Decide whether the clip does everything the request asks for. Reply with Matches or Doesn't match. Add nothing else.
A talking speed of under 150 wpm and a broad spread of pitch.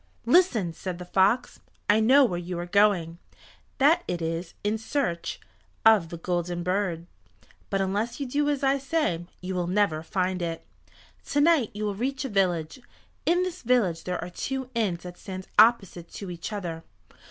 Doesn't match